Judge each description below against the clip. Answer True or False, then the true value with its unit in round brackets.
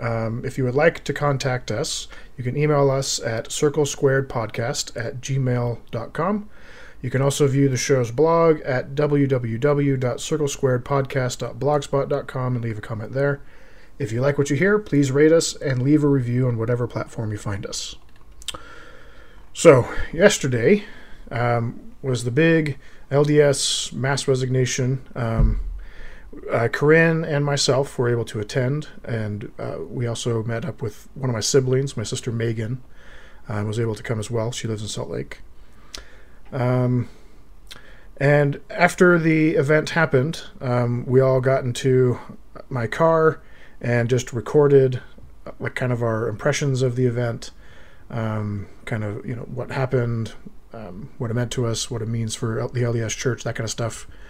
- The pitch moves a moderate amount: True (3.4 semitones)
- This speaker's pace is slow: False (155 wpm)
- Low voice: True (130 Hz)